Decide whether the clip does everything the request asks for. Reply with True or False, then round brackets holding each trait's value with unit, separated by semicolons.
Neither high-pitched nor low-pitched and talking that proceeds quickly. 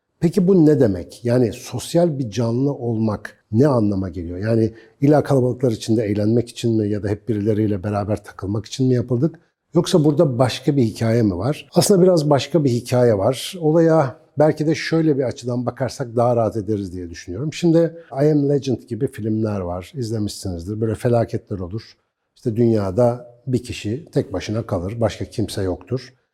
False (120 Hz; 170 wpm)